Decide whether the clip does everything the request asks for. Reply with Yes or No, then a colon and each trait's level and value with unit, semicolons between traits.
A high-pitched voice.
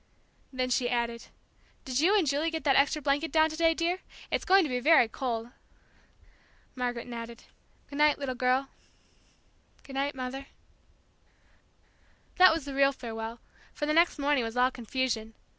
Yes: very high, 270 Hz